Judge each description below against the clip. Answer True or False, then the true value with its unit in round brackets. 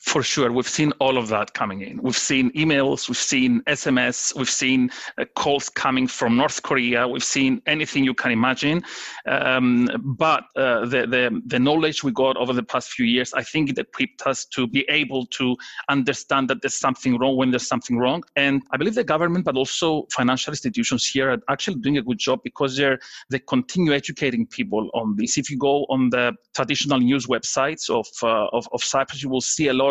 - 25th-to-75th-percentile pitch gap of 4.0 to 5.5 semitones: False (3.2 semitones)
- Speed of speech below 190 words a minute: False (205 wpm)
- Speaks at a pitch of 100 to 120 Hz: False (135 Hz)